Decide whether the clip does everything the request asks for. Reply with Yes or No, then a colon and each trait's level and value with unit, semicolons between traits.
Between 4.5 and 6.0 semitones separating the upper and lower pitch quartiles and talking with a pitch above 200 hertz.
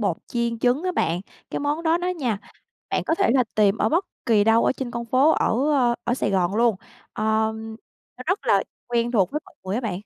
No: average, 4.1 semitones; high, 235 Hz